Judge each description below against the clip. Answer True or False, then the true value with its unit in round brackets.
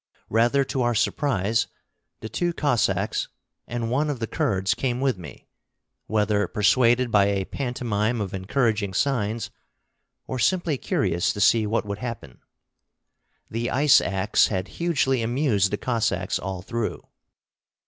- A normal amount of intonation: True (3.9 semitones)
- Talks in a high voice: False (115 Hz)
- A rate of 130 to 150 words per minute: True (140 wpm)